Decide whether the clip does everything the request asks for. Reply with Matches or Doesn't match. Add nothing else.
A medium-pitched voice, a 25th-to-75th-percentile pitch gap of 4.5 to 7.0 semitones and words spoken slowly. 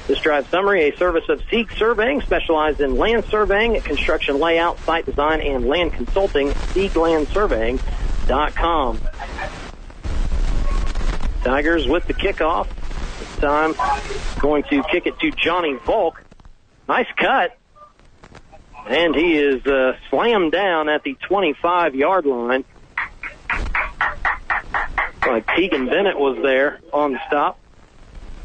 Matches